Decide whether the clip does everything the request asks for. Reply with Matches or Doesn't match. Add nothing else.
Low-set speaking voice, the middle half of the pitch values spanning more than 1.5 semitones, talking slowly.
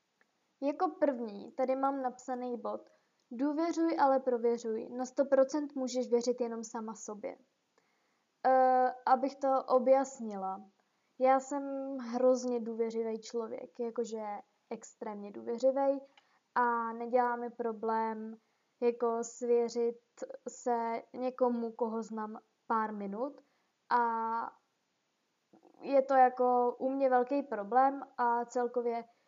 Doesn't match